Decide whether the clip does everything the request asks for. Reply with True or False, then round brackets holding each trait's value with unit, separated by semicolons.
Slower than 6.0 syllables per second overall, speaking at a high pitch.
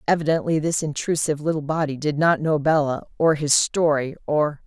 False (5.4 syllables/s; 150 Hz)